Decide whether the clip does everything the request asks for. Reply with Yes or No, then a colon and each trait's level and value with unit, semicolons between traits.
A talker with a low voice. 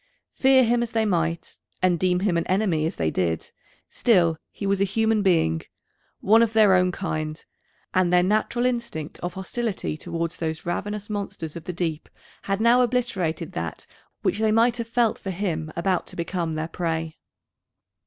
No: medium, 185 Hz